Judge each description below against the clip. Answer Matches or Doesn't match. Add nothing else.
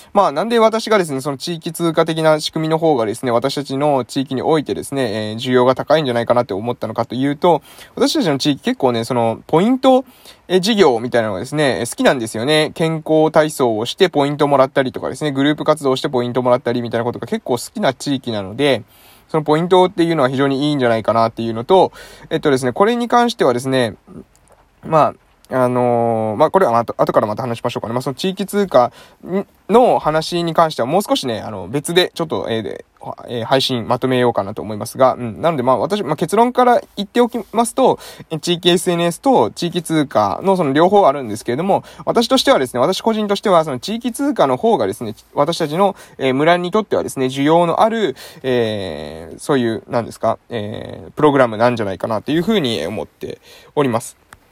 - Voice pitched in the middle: Matches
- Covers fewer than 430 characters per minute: Doesn't match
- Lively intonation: Matches